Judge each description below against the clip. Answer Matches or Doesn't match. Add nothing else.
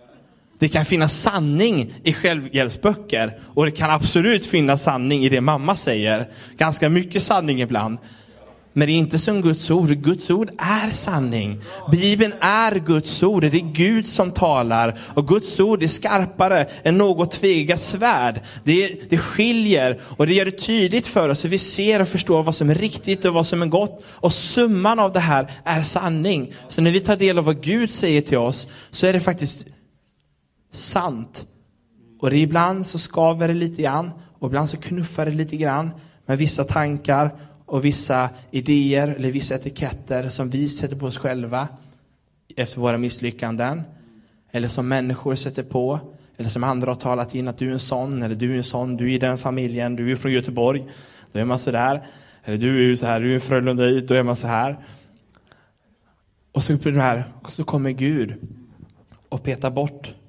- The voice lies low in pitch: Doesn't match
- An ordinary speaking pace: Matches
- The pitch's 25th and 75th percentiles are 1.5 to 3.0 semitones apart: Doesn't match